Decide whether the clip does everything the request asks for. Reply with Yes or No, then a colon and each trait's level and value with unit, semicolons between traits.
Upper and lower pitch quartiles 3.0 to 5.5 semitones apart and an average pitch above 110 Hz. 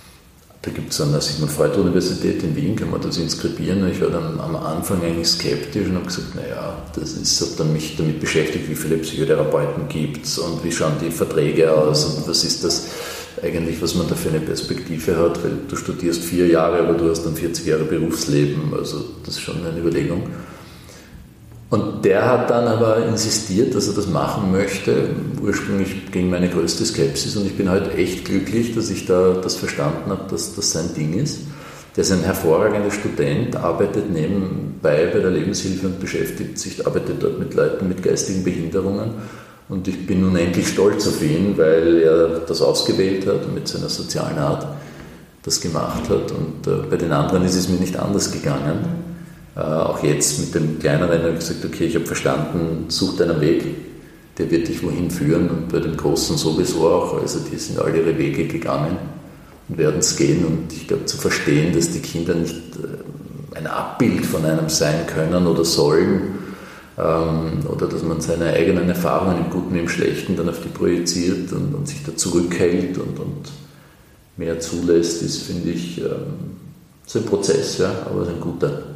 No: average, 3.5 semitones; very low, 90 Hz